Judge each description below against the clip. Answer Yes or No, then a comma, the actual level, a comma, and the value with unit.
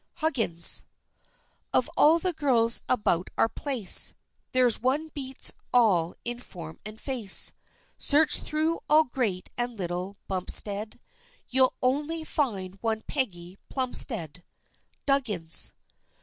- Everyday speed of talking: No, slow, 110 wpm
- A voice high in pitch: Yes, high, 240 Hz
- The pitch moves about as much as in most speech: No, wide, 6.4 semitones